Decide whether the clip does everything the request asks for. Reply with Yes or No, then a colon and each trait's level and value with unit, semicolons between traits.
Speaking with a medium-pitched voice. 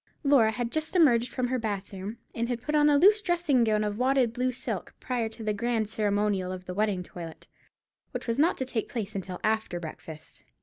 No: high, 230 Hz